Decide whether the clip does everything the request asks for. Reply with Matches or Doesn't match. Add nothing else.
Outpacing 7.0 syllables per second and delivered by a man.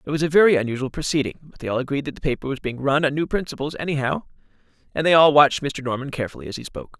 Matches